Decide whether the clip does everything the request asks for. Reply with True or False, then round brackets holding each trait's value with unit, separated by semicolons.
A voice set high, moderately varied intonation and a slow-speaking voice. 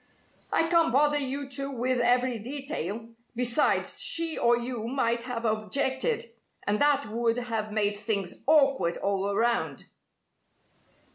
True (245 Hz; 3.9 semitones; 130 wpm)